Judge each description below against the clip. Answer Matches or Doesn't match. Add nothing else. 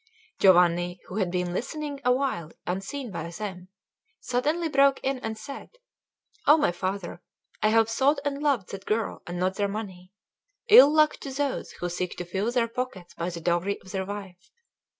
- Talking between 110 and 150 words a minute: Doesn't match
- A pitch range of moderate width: Doesn't match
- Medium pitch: Doesn't match